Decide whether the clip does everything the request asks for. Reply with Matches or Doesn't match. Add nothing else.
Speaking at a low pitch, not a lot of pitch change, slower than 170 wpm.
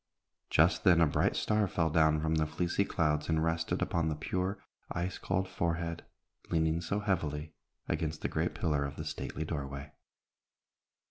Matches